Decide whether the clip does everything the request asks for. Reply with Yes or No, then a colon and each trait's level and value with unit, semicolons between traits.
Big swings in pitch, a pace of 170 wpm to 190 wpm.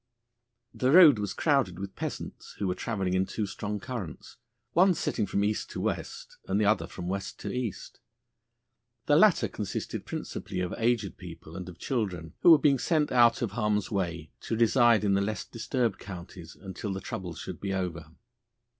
No: average, 4.3 semitones; average, 185 wpm